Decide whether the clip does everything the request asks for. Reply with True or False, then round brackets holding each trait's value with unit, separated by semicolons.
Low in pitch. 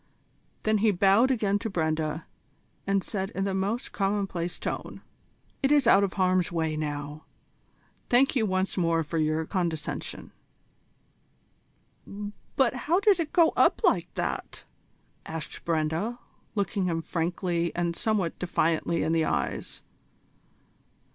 False (185 Hz)